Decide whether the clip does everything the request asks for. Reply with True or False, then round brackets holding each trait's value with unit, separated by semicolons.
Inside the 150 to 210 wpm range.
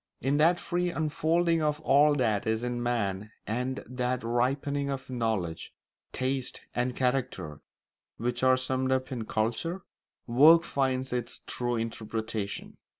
False (135 wpm)